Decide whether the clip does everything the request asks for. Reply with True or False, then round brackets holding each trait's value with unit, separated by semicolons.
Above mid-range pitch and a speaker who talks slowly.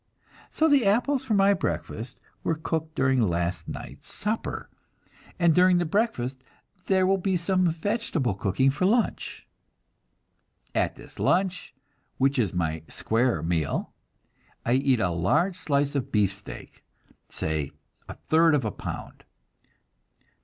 False (145 Hz; 130 wpm)